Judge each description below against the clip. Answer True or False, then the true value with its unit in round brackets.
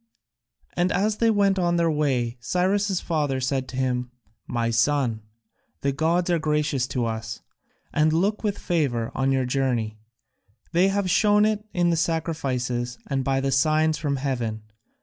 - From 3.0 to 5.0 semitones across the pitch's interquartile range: False (5.6 semitones)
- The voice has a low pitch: False (145 Hz)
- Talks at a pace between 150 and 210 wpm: True (160 wpm)